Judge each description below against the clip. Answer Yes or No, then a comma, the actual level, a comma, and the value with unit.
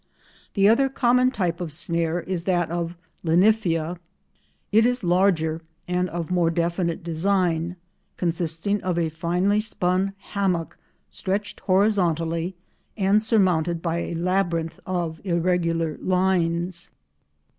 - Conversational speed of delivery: No, slow, 115 wpm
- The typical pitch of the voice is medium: Yes, medium, 175 Hz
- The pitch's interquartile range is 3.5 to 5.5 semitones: No, narrow, 2.6 semitones